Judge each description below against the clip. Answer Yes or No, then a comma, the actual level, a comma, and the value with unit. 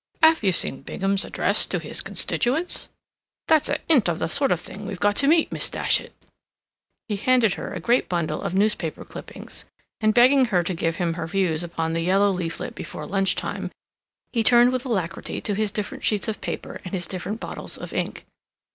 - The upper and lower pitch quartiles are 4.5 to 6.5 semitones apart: Yes, wide, 5.5 semitones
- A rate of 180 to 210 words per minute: Yes, average, 200 wpm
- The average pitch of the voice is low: No, high, 200 Hz